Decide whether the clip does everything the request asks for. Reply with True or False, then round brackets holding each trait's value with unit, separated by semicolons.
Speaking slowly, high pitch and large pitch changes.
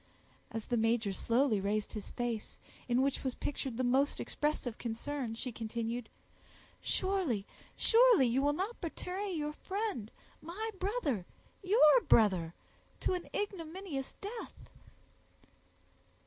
True (110 wpm; 270 Hz; 8.5 semitones)